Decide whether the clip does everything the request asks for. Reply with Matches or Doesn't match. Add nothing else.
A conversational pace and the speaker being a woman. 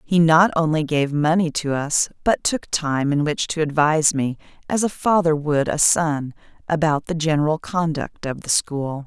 Matches